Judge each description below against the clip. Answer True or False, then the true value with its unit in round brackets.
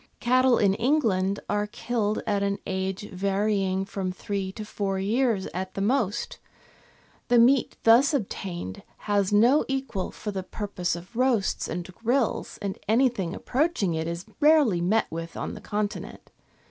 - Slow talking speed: False (150 wpm)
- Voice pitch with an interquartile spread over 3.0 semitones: True (4.0 semitones)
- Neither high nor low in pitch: False (205 Hz)